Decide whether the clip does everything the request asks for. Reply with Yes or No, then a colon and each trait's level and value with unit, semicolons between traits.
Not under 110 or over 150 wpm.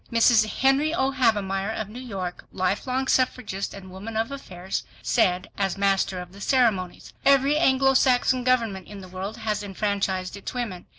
No: average, 170 wpm